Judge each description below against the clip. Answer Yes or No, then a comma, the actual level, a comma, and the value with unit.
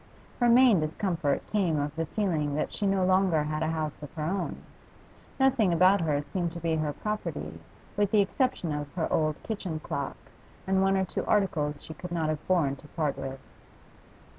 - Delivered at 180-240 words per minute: Yes, average, 190 wpm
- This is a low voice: No, medium, 165 Hz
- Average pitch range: Yes, average, 4.1 semitones